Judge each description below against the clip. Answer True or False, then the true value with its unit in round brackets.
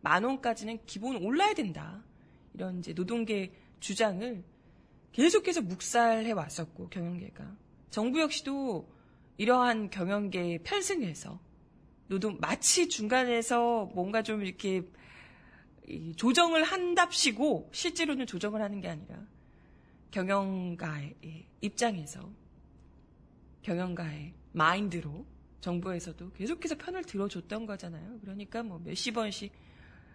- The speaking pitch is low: False (200 Hz)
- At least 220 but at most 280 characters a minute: True (260 characters per minute)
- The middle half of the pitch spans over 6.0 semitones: False (5.3 semitones)